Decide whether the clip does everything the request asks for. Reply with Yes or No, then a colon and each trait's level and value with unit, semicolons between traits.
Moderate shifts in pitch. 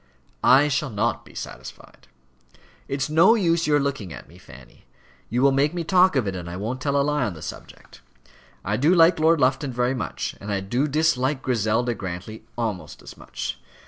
No: wide, 5.9 semitones